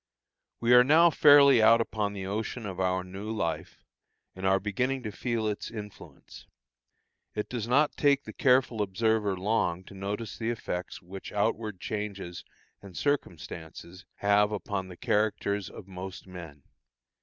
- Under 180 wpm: Yes, average, 150 wpm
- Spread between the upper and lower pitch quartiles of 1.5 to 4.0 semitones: Yes, average, 3.5 semitones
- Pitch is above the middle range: No, low, 105 Hz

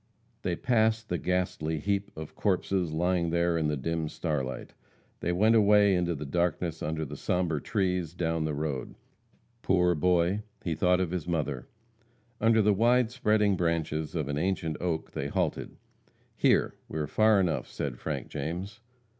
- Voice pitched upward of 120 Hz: No, very low, 85 Hz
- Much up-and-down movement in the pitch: No, average, 3.7 semitones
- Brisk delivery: No, average, 165 wpm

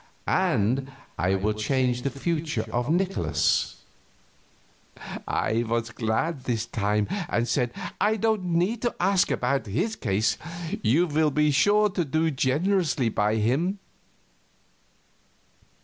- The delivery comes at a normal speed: No, slow, 120 wpm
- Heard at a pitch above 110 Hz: Yes, low, 135 Hz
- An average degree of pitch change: No, wide, 7.4 semitones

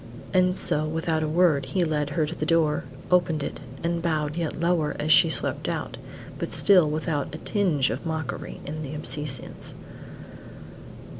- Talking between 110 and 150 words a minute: No, average, 165 wpm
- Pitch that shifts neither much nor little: No, narrow, 2.2 semitones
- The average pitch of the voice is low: No, medium, 155 Hz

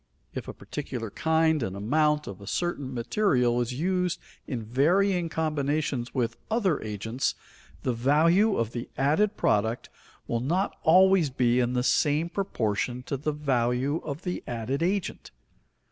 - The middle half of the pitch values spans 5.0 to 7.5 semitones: Yes, wide, 5.5 semitones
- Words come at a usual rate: Yes, average, 145 wpm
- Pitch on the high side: No, medium, 140 Hz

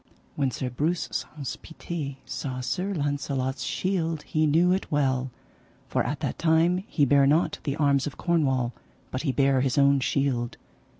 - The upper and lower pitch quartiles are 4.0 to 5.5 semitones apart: No, average, 3.4 semitones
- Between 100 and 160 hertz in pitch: Yes, medium, 140 Hz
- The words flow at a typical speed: Yes, average, 165 wpm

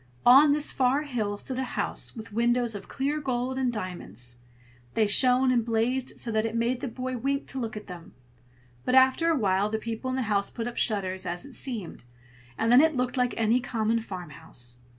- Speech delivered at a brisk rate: Yes, fast, 210 wpm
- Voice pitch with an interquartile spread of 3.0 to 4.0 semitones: Yes, average, 3.7 semitones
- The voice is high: Yes, high, 235 Hz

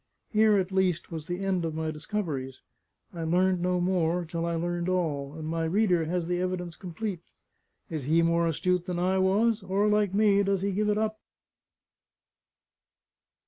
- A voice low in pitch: No, medium, 180 Hz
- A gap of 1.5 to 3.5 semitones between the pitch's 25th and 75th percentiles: Yes, average, 2.8 semitones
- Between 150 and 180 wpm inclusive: Yes, average, 175 wpm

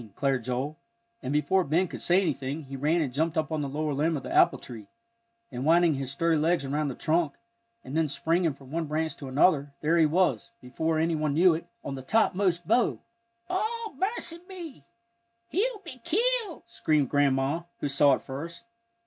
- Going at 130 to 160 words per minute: No, average, 190 wpm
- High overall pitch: No, medium, 155 Hz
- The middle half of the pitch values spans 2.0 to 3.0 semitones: No, average, 4.1 semitones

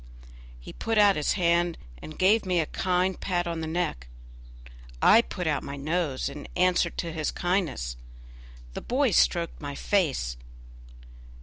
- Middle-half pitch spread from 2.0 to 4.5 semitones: Yes, average, 3.5 semitones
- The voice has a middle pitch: Yes, medium, 170 Hz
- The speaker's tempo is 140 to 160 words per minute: Yes, average, 150 wpm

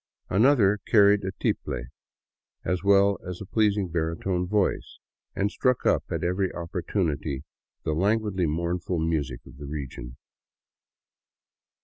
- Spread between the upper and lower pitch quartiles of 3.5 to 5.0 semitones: Yes, average, 3.9 semitones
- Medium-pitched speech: No, very low, 90 Hz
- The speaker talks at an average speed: No, slow, 125 wpm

